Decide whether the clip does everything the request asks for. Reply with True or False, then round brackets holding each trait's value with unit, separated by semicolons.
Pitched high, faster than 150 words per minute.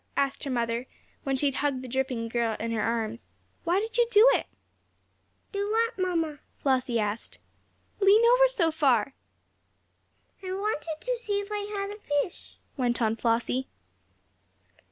True (290 Hz; 160 wpm)